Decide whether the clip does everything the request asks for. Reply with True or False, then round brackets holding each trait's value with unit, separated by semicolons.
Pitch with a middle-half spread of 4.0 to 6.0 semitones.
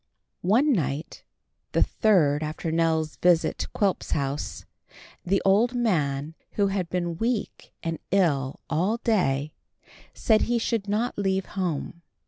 True (5.2 semitones)